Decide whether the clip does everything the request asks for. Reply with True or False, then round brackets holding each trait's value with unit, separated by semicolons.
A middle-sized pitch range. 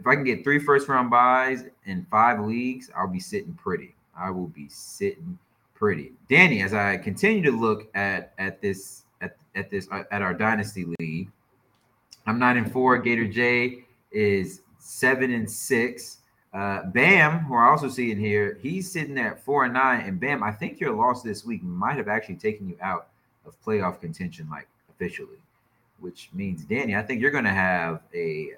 False (6.7 semitones)